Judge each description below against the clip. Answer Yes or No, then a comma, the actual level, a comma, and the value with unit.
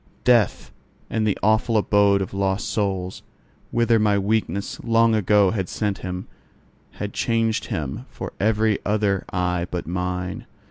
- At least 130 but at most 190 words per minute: Yes, average, 140 wpm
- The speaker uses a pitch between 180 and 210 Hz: No, low, 100 Hz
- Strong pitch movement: No, average, 2.8 semitones